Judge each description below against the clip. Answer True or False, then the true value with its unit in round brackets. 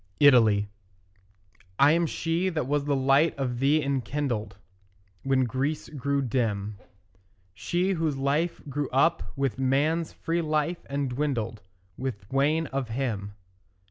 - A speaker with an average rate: False (130 wpm)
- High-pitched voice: False (140 Hz)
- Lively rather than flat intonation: False (3.6 semitones)